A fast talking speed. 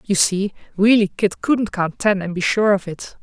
Yes: fast, 225 wpm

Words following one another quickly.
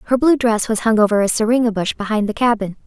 Yes: fast, 250 wpm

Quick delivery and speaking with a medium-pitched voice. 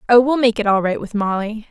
No: fast, 280 wpm; high, 225 Hz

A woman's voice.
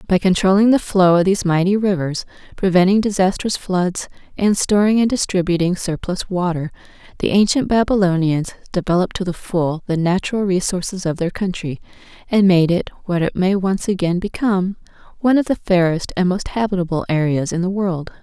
Yes: female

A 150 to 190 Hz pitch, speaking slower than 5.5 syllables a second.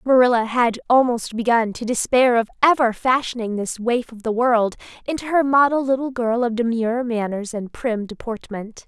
No: high, 235 Hz; 5.0 syllables/s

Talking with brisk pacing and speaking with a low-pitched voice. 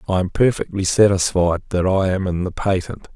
No: average, 190 wpm; very low, 95 Hz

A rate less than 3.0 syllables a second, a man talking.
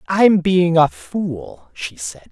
Yes: 2.8 syllables/s; male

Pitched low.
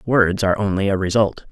Yes: low, 100 Hz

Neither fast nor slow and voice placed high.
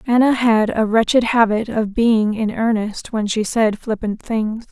Yes: average, 180 wpm; high, 220 Hz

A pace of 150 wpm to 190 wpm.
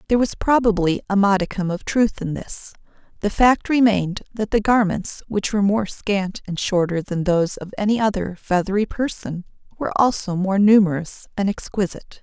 Yes: average, 160 wpm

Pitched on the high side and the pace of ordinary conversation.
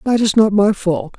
No: high, 200 Hz; fast, 250 wpm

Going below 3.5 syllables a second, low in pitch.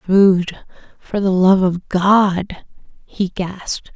No: 2.8 syllables/s; high, 190 Hz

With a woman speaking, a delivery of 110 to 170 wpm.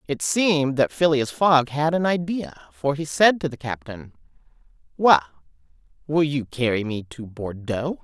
Yes: female; average, 155 wpm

